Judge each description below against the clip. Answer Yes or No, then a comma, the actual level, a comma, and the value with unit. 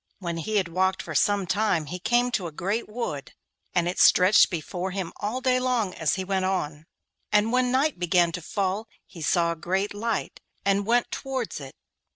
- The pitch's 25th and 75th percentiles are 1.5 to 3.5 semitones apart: No, average, 4.1 semitones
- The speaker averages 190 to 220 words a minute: Yes, average, 195 wpm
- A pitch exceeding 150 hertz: Yes, high, 190 Hz